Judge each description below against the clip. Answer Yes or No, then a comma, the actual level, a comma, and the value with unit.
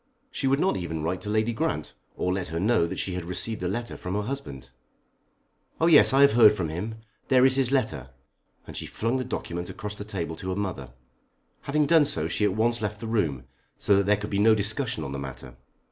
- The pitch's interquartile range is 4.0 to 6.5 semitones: Yes, average, 5.2 semitones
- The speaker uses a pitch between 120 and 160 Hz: No, low, 105 Hz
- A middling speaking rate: No, fast, 235 wpm